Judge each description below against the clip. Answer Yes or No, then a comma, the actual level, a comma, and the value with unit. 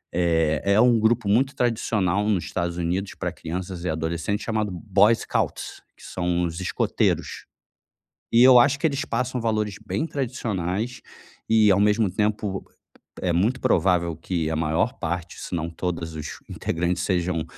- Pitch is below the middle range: Yes, very low, 95 Hz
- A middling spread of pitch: Yes, average, 4.5 semitones